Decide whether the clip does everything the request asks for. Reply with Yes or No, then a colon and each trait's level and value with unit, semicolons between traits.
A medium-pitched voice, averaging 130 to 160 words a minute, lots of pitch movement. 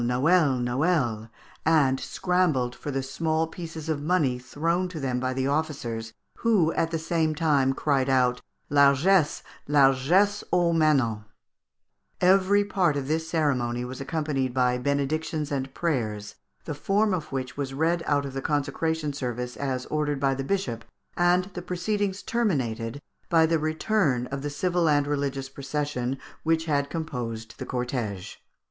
No: medium, 145 Hz; average, 150 wpm; average, 4.0 semitones